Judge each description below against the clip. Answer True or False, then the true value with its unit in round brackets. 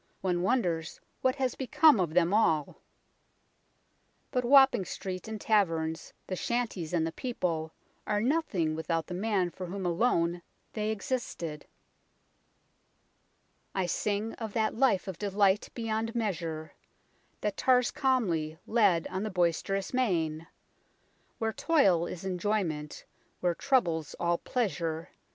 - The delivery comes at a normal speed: False (130 wpm)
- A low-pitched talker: False (190 Hz)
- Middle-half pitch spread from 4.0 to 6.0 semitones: True (5.1 semitones)